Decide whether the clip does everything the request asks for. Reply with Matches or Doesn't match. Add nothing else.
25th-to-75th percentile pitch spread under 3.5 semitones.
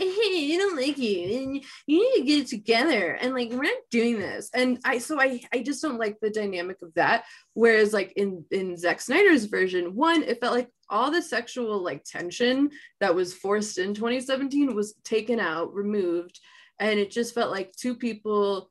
Doesn't match